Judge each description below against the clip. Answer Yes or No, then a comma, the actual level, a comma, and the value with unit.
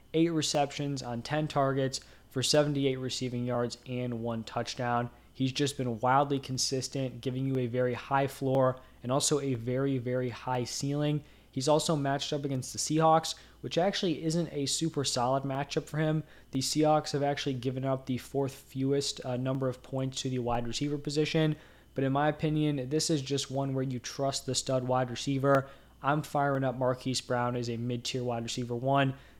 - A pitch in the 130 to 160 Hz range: Yes, low, 135 Hz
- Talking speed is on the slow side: No, average, 185 wpm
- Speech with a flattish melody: Yes, narrow, 2.3 semitones